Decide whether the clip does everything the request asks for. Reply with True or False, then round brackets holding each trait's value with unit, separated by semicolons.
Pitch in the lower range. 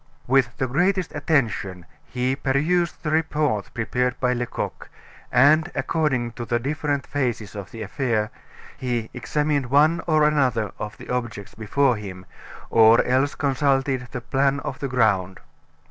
True (130 Hz)